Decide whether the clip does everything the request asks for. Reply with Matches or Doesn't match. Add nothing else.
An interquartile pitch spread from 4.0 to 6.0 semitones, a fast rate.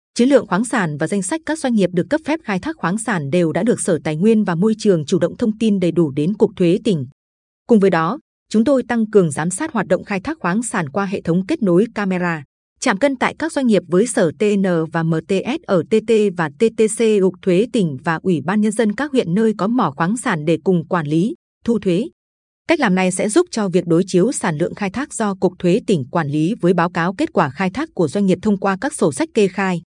Matches